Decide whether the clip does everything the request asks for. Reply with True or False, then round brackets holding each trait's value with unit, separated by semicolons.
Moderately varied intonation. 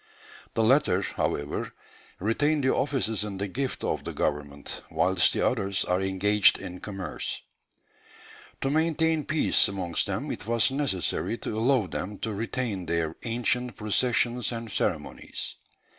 True (5.0 semitones)